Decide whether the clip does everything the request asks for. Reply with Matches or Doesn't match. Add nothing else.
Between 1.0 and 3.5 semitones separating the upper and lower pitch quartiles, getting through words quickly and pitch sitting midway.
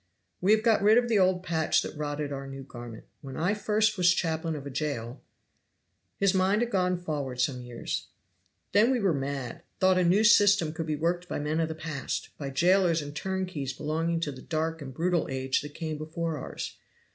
Doesn't match